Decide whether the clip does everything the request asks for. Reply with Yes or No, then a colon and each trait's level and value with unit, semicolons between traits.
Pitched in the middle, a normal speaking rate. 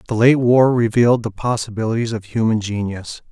No: low, 115 Hz; average, 165 wpm